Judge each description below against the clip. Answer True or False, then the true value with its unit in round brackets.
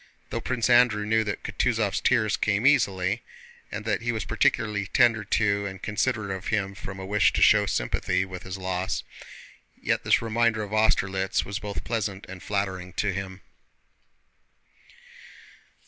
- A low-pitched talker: True (100 Hz)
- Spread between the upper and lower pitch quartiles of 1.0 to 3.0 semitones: True (2.6 semitones)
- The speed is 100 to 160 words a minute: True (155 wpm)